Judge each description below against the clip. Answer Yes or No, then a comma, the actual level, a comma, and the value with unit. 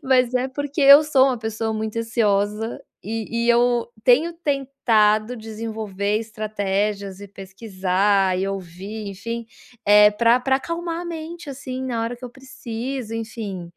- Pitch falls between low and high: No, high, 225 Hz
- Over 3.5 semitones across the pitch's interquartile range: Yes, average, 3.9 semitones